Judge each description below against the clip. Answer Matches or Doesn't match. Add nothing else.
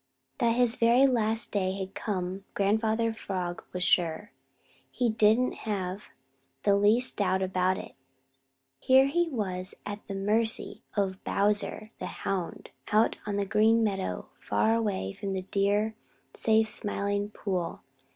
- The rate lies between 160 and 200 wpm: Doesn't match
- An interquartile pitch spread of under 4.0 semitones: Matches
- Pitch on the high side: Matches